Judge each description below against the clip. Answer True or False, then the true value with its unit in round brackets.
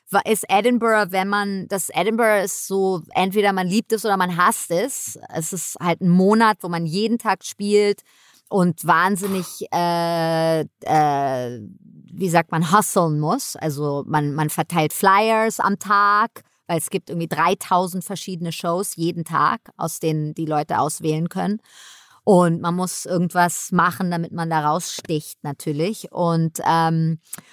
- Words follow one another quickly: False (150 wpm)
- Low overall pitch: False (180 Hz)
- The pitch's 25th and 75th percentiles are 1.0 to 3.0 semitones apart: False (3.4 semitones)